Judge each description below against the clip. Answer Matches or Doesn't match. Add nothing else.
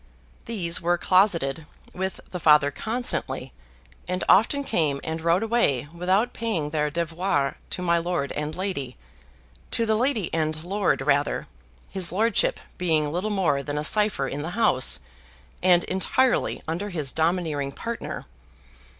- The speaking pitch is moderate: Matches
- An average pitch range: Matches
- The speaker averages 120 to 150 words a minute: Matches